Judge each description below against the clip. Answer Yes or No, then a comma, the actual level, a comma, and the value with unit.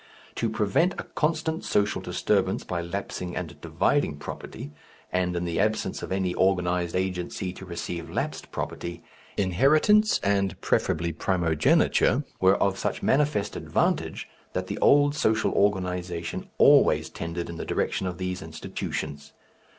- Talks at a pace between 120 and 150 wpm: Yes, slow, 135 wpm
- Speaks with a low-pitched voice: Yes, very low, 95 Hz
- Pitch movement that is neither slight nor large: Yes, average, 3.0 semitones